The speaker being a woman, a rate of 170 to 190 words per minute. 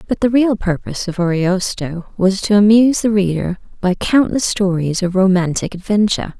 No: female; average, 160 wpm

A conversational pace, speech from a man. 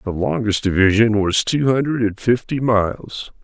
Yes: average, 155 wpm; male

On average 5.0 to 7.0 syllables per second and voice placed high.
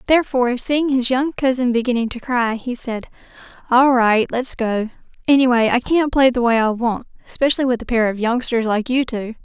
Yes: 5.4 syllables/s; high, 245 Hz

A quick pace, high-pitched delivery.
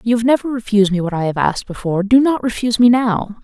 Yes: fast, 260 wpm; high, 220 Hz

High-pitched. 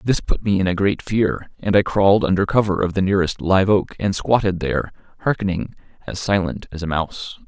No: very low, 95 Hz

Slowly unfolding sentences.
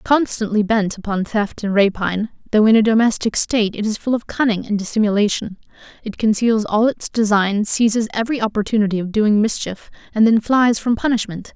No: average, 175 wpm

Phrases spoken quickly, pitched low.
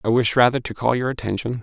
Yes: fast, 260 wpm; low, 120 Hz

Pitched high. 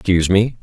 No: very low, 95 Hz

